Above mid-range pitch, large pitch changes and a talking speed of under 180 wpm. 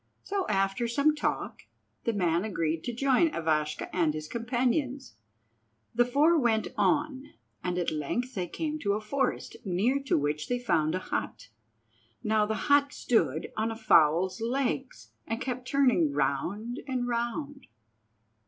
Yes: high, 230 Hz; wide, 7.2 semitones; average, 150 wpm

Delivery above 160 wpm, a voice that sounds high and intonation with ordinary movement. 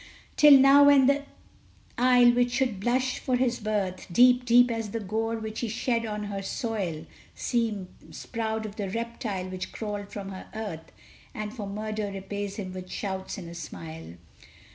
Yes: average, 170 wpm; high, 215 Hz; average, 3.6 semitones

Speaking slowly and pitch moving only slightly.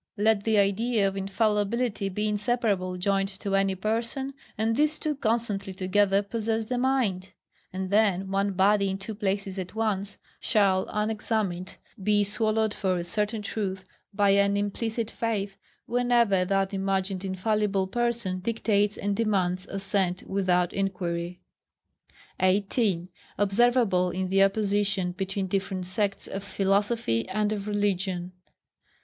Yes: slow, 130 wpm; narrow, 2.2 semitones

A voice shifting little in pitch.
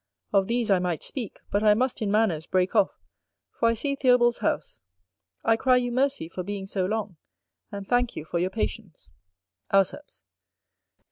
No: average, 4.4 semitones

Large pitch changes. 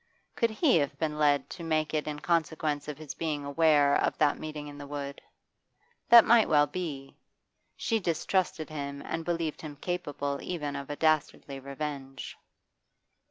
No: narrow, 2.4 semitones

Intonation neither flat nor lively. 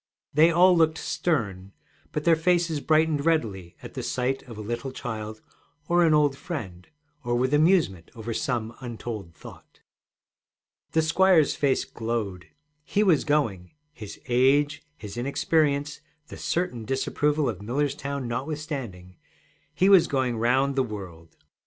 No: wide, 5.7 semitones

